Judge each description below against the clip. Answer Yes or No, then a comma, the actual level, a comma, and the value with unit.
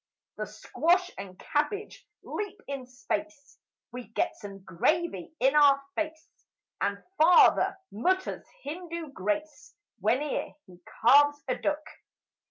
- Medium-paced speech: No, slow, 115 wpm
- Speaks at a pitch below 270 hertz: No, very high, 290 Hz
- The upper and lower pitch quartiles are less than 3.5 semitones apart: No, average, 4.8 semitones